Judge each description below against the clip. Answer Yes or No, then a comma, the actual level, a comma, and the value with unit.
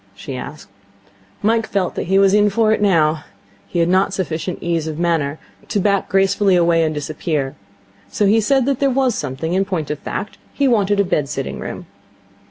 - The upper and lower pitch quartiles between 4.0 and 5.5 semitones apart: Yes, average, 4.6 semitones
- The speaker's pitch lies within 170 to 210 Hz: Yes, medium, 185 Hz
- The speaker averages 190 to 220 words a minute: Yes, average, 195 wpm